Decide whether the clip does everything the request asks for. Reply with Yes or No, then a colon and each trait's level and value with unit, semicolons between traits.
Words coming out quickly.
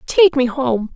No: average, 190 wpm